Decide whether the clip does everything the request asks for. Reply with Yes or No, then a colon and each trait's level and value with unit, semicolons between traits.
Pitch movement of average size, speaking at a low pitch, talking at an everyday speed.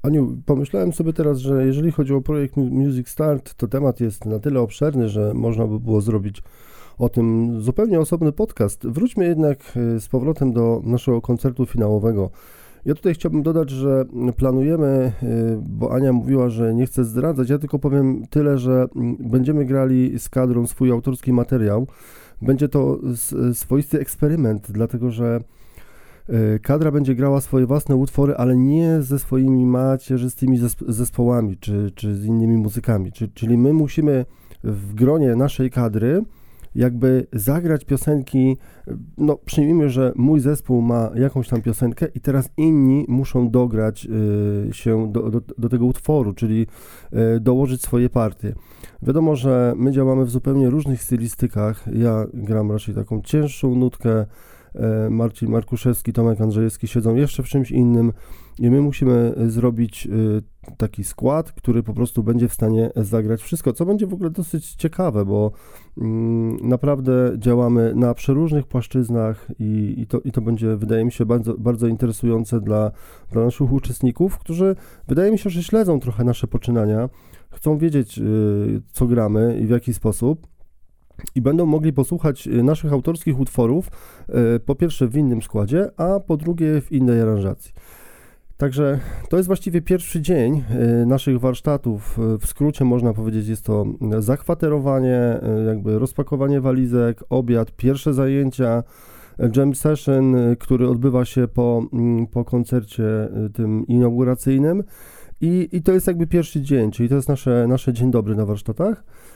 Yes: average, 3.4 semitones; low, 125 Hz; average, 145 wpm